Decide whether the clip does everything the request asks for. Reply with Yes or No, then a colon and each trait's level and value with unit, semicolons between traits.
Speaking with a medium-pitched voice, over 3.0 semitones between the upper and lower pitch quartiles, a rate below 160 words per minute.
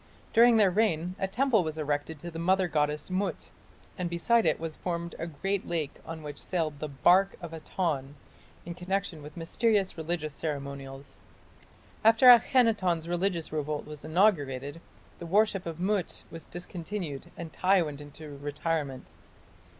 Yes: medium, 170 Hz; average, 4.2 semitones; average, 150 wpm